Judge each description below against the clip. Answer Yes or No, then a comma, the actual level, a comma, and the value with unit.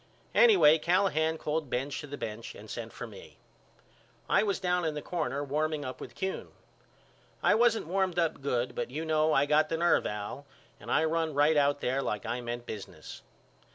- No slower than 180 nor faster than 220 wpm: Yes, average, 190 wpm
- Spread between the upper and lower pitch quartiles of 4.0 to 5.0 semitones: No, average, 3.4 semitones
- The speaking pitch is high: No, medium, 155 Hz